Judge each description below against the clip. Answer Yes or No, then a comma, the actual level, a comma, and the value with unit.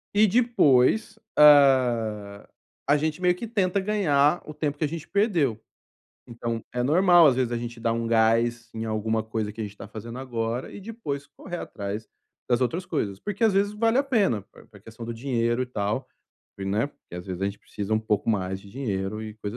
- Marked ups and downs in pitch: Yes, wide, 6.7 semitones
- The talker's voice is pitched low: Yes, low, 120 Hz